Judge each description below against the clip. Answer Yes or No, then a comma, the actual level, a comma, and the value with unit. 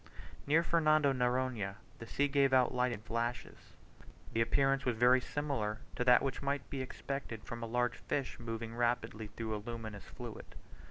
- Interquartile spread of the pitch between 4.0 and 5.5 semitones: No, average, 3.1 semitones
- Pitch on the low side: Yes, low, 125 Hz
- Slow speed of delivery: No, average, 170 wpm